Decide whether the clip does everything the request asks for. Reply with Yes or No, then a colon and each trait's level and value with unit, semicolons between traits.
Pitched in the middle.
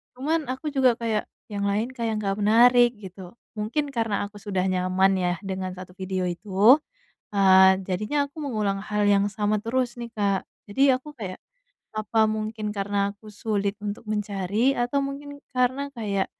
No: high, 210 Hz